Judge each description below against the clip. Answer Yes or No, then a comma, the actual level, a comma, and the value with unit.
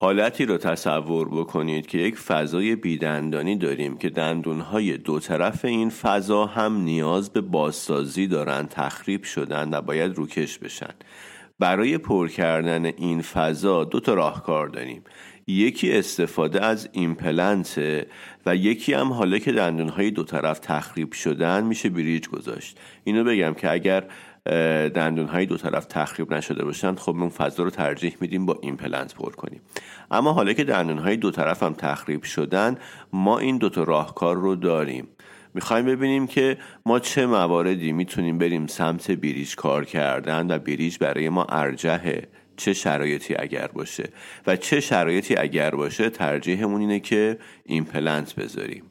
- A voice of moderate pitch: No, very low, 85 Hz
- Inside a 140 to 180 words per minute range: Yes, average, 145 wpm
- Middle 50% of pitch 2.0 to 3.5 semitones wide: No, average, 4.1 semitones